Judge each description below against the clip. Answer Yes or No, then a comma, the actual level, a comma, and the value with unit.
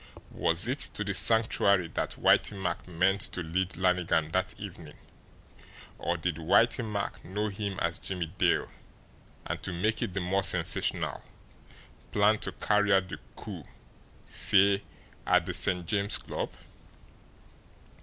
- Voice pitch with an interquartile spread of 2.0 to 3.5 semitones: Yes, narrow, 2.6 semitones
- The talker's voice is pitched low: Yes, very low, 95 Hz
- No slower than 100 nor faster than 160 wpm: Yes, average, 140 wpm